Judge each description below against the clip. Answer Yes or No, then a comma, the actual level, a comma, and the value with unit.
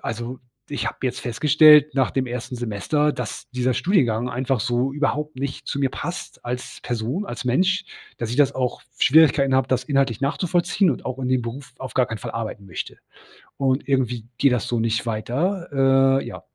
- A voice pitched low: Yes, low, 130 Hz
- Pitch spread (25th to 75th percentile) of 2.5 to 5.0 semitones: Yes, average, 2.9 semitones